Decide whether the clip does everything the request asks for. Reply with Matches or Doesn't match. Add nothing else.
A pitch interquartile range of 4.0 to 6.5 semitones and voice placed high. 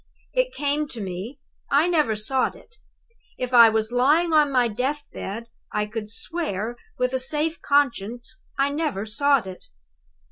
Matches